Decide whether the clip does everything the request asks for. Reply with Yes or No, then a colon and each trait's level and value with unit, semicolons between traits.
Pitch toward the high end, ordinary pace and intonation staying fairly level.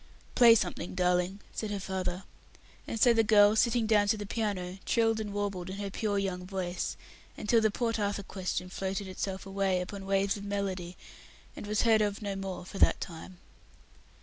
Yes: high, 200 Hz; average, 185 wpm; narrow, 2.1 semitones